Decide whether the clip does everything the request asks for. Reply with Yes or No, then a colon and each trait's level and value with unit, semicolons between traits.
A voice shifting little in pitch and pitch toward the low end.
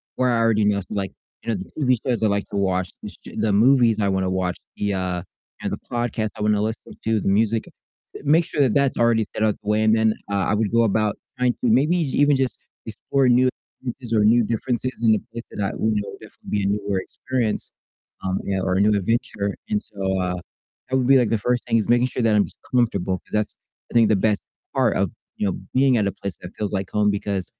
No: average, 3.2 semitones; low, 110 Hz